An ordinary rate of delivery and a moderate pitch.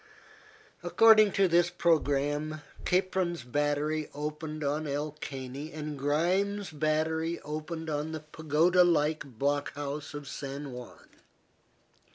No: slow, 115 wpm; medium, 155 Hz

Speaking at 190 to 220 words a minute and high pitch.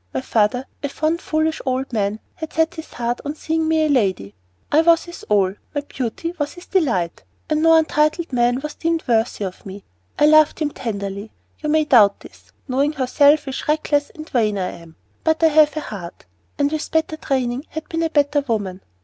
Yes: average, 200 wpm; very high, 285 Hz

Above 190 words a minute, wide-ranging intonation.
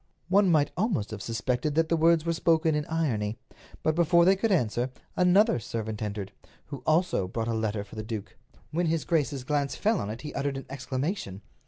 Yes: average, 200 wpm; wide, 7.0 semitones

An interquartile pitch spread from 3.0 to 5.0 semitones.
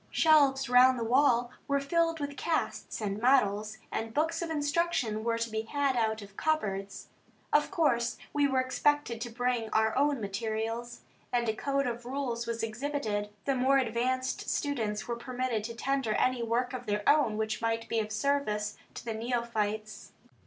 Yes: average, 3.9 semitones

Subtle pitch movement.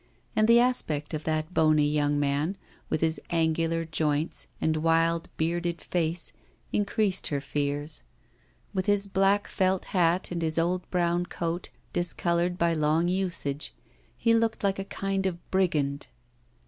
No: average, 3.2 semitones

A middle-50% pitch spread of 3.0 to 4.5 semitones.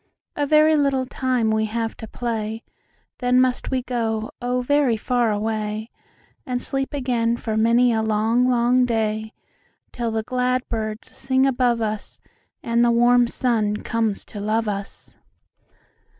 No: narrow, 2.4 semitones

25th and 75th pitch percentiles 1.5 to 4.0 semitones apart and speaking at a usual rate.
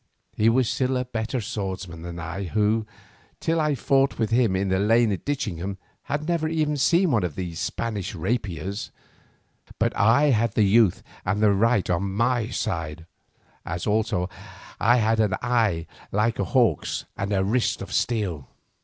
No: average, 4.4 semitones; average, 170 wpm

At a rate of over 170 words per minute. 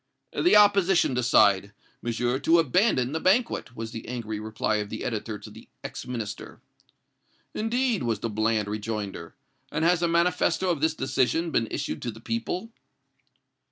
No: average, 155 wpm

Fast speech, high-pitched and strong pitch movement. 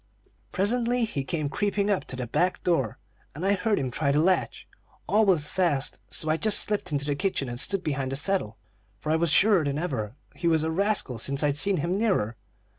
No: fast, 215 wpm; medium, 160 Hz; wide, 5.9 semitones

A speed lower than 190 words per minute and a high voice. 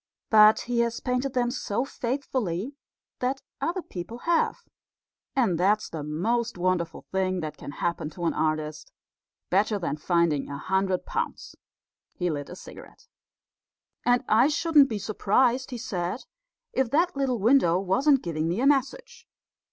Yes: average, 150 wpm; high, 215 Hz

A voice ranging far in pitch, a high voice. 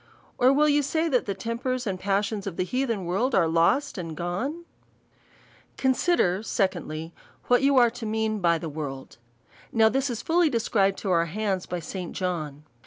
Yes: wide, 6.3 semitones; high, 205 Hz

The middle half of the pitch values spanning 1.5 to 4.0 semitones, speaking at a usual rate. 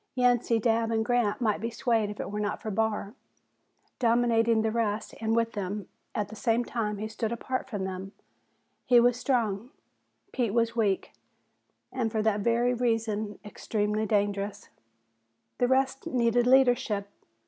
Yes: narrow, 2.4 semitones; average, 155 wpm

